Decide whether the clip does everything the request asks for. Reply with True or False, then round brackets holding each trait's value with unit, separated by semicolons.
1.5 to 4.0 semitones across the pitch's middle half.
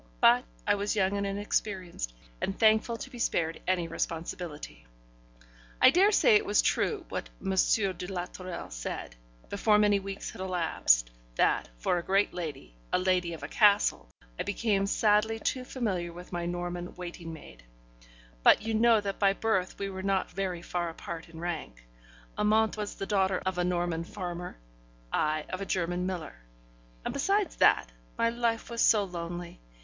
True (3.3 semitones)